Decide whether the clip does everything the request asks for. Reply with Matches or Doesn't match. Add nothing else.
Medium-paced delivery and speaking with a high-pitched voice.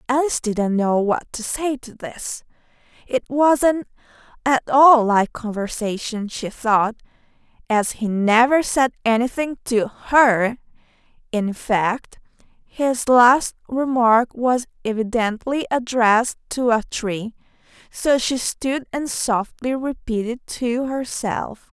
Doesn't match